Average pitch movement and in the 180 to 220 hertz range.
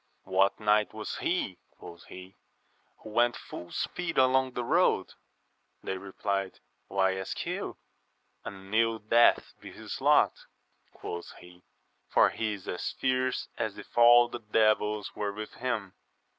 No: average, 3.7 semitones; low, 105 Hz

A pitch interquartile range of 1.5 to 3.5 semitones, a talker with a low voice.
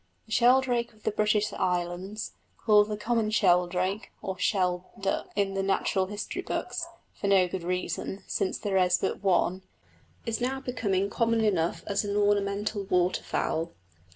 No: average, 2.7 semitones; high, 200 Hz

